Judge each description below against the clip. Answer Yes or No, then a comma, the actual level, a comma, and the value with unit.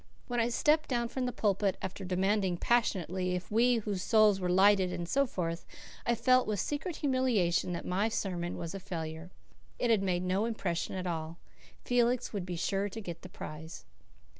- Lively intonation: No, average, 4.6 semitones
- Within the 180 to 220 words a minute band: Yes, average, 190 wpm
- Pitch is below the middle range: No, high, 195 Hz